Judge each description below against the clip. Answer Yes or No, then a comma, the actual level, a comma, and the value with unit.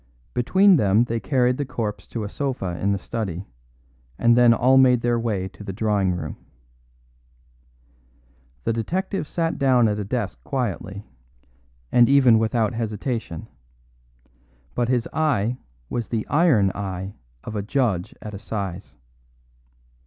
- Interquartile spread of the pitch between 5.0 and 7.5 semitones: No, average, 3.8 semitones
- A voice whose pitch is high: No, low, 115 Hz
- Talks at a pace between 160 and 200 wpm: No, average, 140 wpm